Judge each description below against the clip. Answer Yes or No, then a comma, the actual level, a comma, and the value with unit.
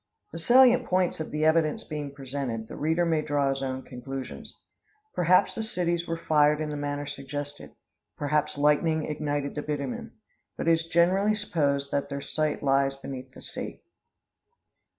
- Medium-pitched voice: Yes, medium, 150 Hz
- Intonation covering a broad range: No, average, 2.9 semitones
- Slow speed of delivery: No, average, 165 wpm